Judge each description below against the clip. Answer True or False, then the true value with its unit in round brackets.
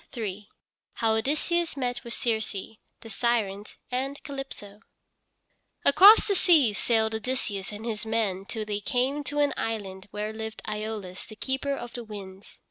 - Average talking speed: True (150 wpm)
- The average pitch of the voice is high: True (225 Hz)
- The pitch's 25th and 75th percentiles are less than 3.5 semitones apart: False (4.1 semitones)